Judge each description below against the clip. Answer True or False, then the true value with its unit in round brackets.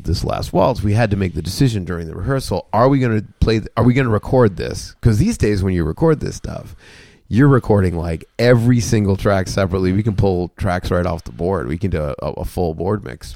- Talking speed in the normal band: False (245 wpm)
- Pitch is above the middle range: False (105 Hz)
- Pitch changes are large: False (4.5 semitones)